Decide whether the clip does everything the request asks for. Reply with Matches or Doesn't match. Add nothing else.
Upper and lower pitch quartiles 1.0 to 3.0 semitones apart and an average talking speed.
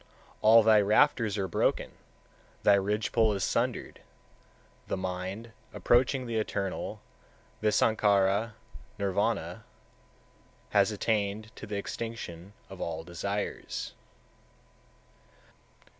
Doesn't match